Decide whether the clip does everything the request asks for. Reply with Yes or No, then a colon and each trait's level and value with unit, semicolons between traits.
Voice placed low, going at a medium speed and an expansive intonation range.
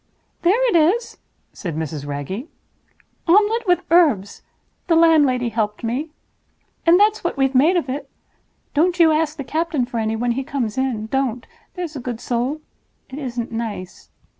No: very high, 270 Hz; average, 160 wpm; wide, 6.1 semitones